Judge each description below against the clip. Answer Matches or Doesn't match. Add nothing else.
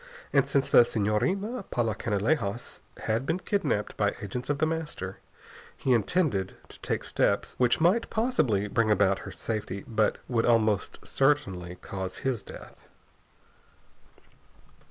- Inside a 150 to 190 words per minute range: Doesn't match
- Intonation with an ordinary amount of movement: Doesn't match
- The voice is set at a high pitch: Doesn't match